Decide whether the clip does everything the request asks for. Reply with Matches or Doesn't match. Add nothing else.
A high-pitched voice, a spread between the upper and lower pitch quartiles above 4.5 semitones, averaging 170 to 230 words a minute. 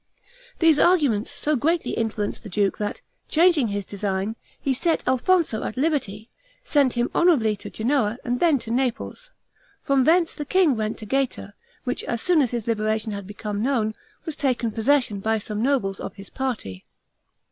Matches